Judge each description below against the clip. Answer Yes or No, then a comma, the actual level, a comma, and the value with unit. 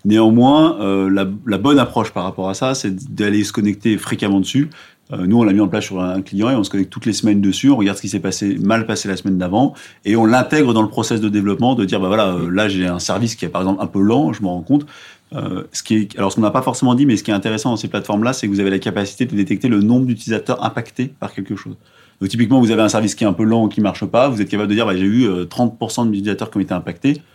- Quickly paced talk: Yes, fast, 305 wpm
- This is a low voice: Yes, low, 105 Hz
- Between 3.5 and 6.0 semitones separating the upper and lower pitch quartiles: No, average, 3.1 semitones